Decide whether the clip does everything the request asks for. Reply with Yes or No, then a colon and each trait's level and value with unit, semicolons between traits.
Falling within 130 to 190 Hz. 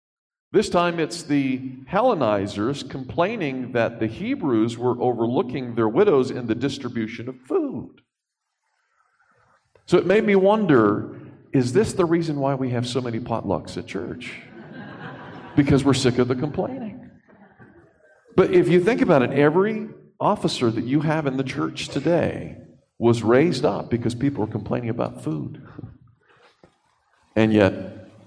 Yes: low, 135 Hz